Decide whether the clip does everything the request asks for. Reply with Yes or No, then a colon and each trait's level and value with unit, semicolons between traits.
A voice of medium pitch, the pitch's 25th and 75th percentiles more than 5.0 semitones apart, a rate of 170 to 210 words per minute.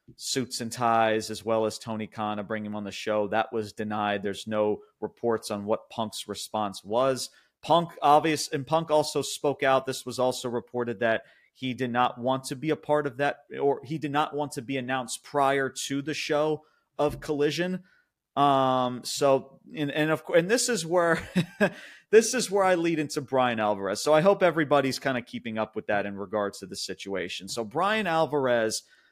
No: low, 130 Hz; wide, 5.5 semitones; average, 200 wpm